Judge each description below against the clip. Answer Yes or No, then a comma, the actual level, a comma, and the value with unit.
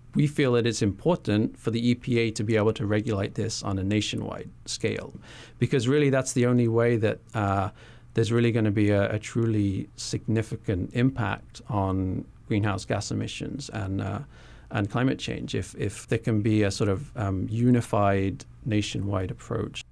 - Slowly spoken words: No, average, 170 wpm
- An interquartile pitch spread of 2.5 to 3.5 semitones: Yes, average, 2.8 semitones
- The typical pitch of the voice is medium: No, low, 110 Hz